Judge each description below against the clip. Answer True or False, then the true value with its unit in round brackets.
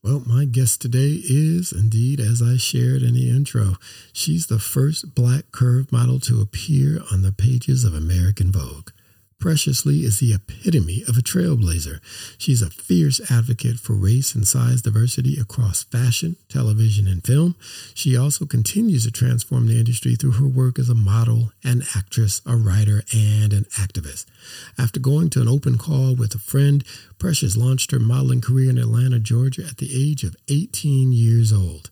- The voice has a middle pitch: False (120 Hz)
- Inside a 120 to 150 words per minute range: False (175 wpm)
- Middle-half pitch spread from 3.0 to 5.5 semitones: True (3.6 semitones)